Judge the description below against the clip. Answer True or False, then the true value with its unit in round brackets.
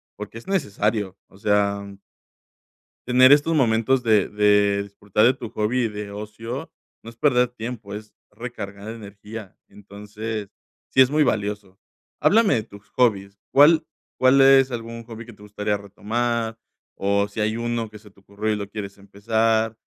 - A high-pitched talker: False (110 Hz)